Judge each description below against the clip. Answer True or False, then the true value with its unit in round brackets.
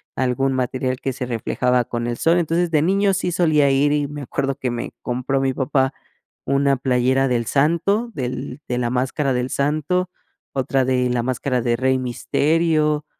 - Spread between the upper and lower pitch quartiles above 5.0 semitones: False (3.2 semitones)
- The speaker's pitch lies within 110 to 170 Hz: True (135 Hz)